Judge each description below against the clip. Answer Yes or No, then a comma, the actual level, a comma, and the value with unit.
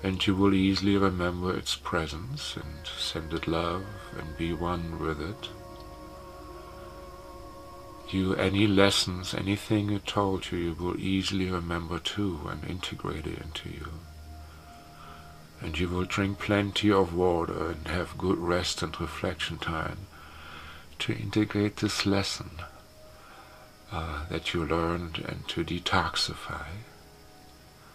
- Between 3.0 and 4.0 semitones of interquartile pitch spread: Yes, average, 3.7 semitones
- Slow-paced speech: Yes, slow, 125 wpm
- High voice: No, very low, 90 Hz